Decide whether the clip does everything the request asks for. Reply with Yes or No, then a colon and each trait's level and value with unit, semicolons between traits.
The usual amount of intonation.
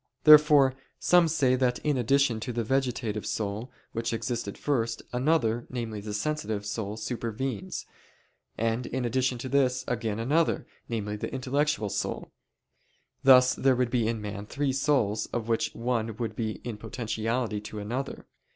Yes: average, 3.1 semitones